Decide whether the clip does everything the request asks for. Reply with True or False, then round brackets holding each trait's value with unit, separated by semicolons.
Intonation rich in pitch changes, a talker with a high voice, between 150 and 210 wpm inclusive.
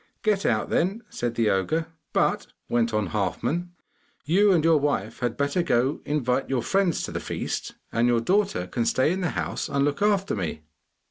False (7.3 semitones; 140 Hz; 195 wpm)